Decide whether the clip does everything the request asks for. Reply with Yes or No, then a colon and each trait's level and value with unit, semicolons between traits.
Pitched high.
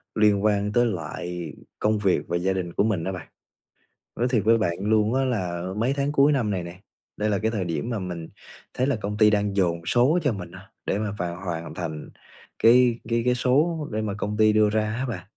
No: low, 105 Hz